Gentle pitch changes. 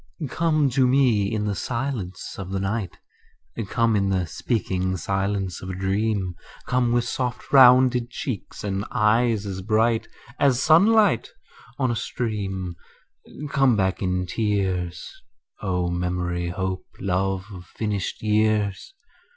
No: average, 4.2 semitones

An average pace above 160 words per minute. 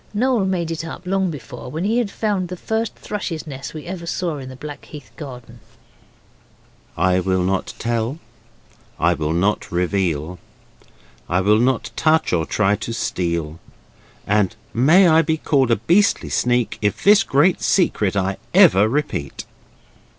No: average, 155 wpm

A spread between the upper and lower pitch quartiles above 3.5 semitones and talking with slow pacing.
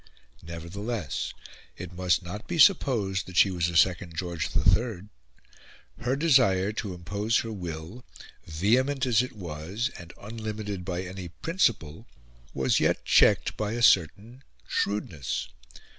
Yes: average, 4.9 semitones; slow, 130 wpm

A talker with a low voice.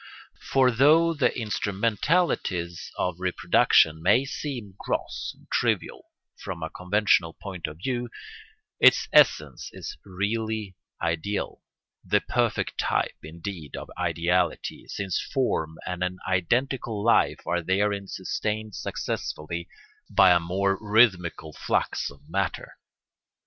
Yes: very low, 95 Hz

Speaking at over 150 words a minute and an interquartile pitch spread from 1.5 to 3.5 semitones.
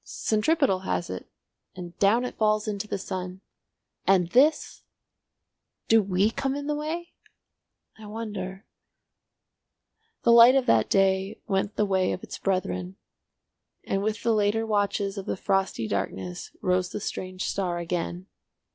No: average, 145 wpm; average, 3.1 semitones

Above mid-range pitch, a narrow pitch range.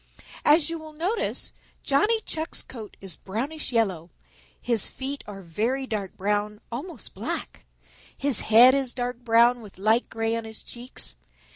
No: high, 235 Hz; average, 4.7 semitones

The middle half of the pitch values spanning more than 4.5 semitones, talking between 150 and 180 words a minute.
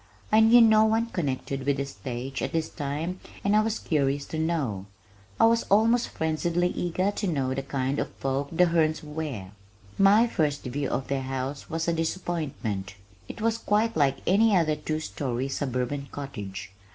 Yes: wide, 5.4 semitones; average, 175 wpm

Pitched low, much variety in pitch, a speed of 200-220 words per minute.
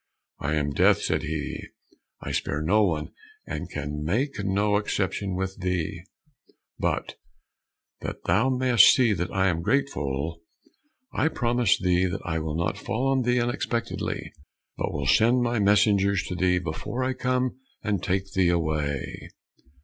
No: very low, 95 Hz; wide, 6.2 semitones; average, 150 wpm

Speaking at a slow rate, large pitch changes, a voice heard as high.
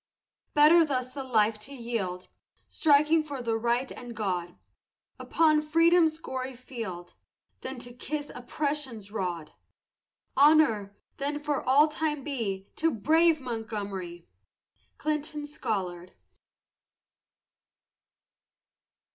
Yes: slow, 105 wpm; wide, 6.0 semitones; very high, 255 Hz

